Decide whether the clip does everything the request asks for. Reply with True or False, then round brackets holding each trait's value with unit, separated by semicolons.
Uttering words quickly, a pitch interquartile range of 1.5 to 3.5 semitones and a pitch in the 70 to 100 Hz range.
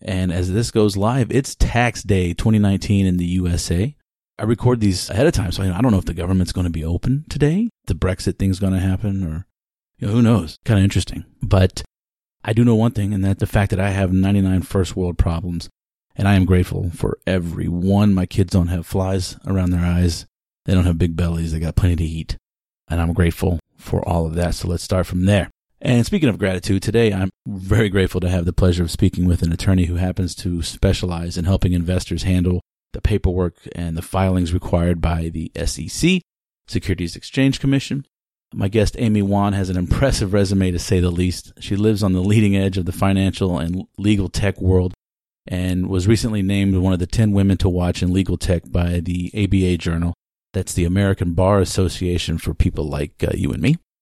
True (210 wpm; 2.5 semitones; 95 Hz)